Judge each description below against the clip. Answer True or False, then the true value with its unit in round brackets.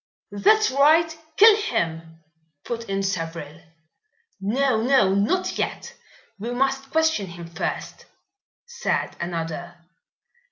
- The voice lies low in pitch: False (215 Hz)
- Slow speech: True (105 wpm)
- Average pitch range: False (8.5 semitones)